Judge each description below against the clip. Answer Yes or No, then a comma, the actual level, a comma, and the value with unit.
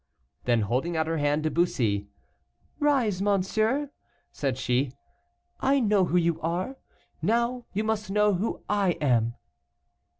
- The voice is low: No, medium, 180 Hz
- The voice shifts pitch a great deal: Yes, wide, 6.9 semitones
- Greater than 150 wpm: No, slow, 135 wpm